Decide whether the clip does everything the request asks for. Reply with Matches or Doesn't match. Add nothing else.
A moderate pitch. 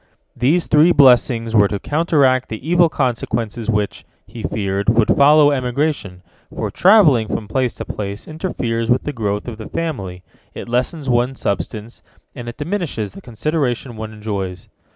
Doesn't match